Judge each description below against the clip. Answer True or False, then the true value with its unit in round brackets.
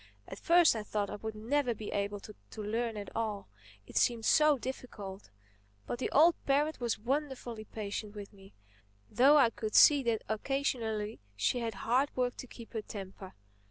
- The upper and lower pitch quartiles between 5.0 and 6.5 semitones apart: False (4.0 semitones)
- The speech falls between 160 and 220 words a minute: True (165 wpm)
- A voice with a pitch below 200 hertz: False (220 Hz)